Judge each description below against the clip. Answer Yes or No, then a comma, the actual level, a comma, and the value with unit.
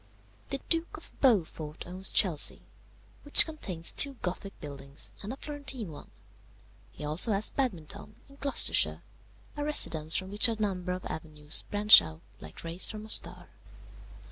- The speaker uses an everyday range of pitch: No, wide, 7.6 semitones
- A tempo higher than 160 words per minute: No, average, 150 wpm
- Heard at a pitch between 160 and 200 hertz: Yes, high, 190 Hz